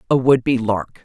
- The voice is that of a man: No, female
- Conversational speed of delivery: No, fast, 230 wpm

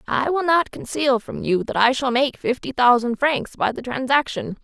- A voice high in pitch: Yes, very high, 255 Hz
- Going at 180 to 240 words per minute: Yes, fast, 205 wpm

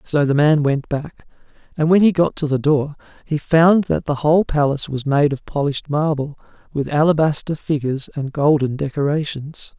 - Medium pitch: Yes, medium, 150 Hz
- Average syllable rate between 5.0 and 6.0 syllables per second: Yes, 5.2 syllables/s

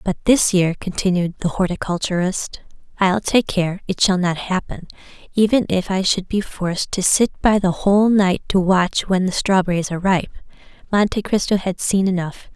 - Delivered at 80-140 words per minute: No, average, 175 wpm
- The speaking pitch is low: No, high, 190 Hz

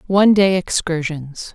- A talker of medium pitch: Yes, medium, 175 Hz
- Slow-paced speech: Yes, slow, 115 wpm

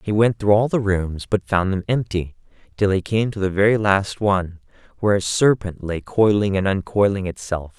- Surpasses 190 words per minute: Yes, average, 200 wpm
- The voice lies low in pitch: Yes, low, 100 Hz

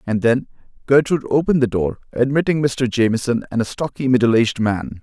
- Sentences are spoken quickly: No, average, 180 wpm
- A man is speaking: Yes, male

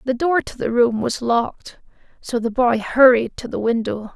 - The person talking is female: Yes, female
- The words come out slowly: No, average, 200 wpm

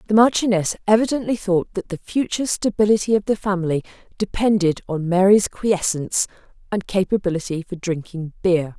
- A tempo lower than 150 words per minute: Yes, slow, 135 wpm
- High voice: Yes, high, 195 Hz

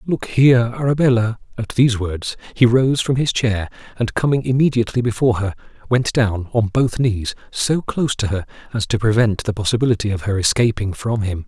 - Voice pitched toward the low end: Yes, low, 115 Hz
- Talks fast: No, average, 185 wpm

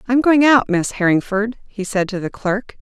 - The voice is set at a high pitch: Yes, high, 215 Hz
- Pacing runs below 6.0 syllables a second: Yes, 5.2 syllables/s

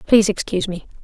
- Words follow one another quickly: No, average, 175 wpm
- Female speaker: Yes, female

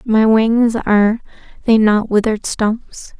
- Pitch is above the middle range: Yes, high, 220 Hz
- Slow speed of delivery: Yes, slow, 130 wpm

